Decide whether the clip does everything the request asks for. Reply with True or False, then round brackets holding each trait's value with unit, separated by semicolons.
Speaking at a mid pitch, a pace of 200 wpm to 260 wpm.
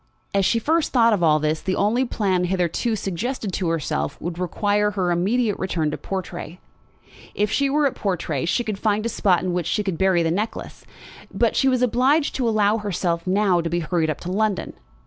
False (195 Hz; 205 wpm)